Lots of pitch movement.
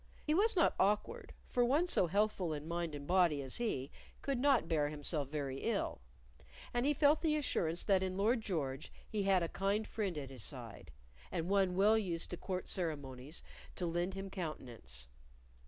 Yes: wide, 6.0 semitones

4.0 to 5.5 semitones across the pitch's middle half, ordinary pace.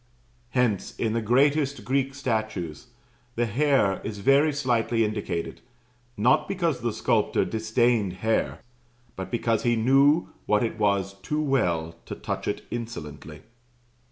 No: average, 4.7 semitones; slow, 130 wpm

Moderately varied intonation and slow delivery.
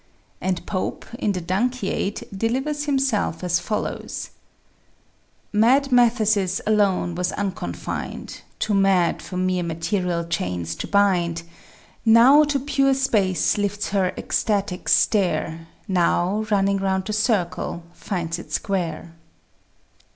Yes: average, 3.6 semitones; slow, 115 wpm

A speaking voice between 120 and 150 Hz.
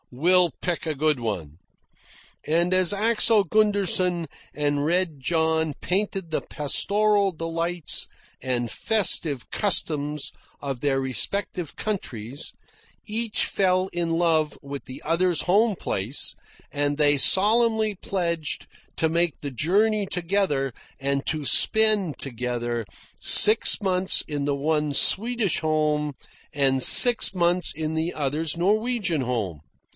No: medium, 165 Hz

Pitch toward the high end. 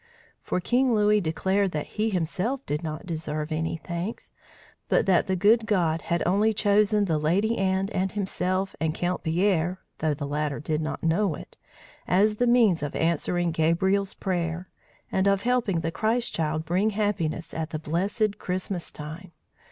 No: medium, 180 Hz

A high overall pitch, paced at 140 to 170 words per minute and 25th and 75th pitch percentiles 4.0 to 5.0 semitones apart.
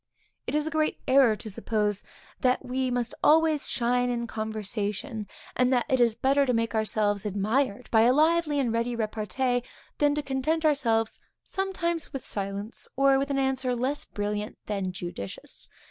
Yes: high, 245 Hz; average, 165 wpm; average, 4.3 semitones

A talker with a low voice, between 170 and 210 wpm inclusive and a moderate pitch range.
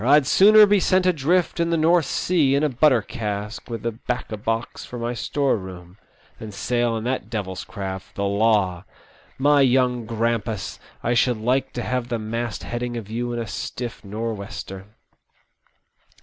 Yes: low, 120 Hz; average, 175 wpm; average, 3.7 semitones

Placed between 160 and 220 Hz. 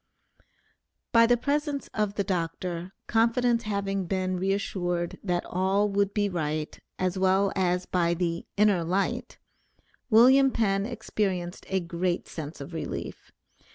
Yes: high, 190 Hz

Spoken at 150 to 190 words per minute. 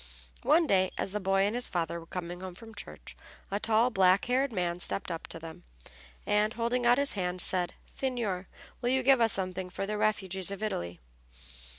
No: average, 200 wpm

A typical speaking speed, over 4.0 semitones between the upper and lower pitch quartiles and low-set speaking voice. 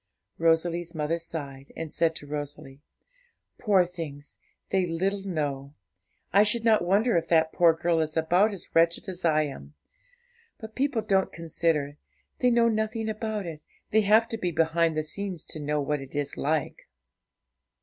No: average, 165 wpm; average, 4.7 semitones; medium, 165 Hz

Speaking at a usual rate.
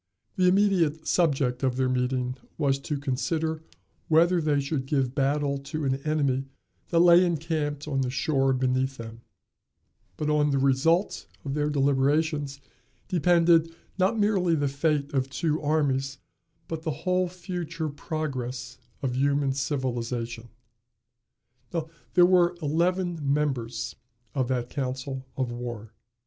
No: slow, 130 wpm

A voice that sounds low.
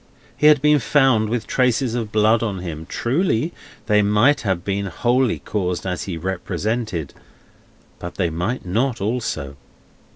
Yes: low, 110 Hz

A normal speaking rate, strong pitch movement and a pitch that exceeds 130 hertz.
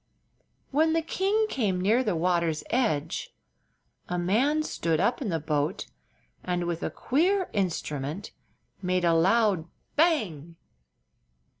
No: slow, 125 wpm; wide, 8.1 semitones; medium, 185 Hz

